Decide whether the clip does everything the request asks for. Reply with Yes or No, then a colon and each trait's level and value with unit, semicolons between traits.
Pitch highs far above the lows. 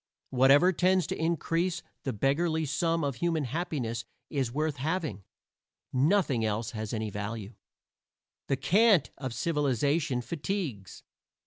Yes: wide, 5.9 semitones